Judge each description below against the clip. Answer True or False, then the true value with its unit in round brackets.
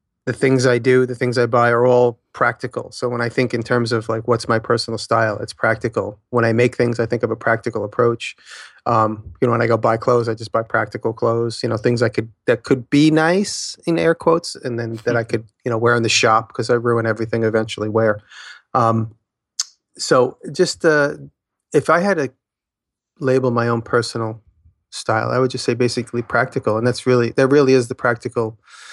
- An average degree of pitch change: False (1.8 semitones)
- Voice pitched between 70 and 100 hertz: False (120 Hz)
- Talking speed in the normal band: False (220 wpm)